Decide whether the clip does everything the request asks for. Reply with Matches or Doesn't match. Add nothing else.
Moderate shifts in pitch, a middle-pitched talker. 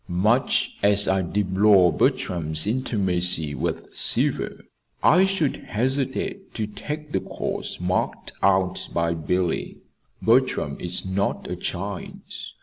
Doesn't match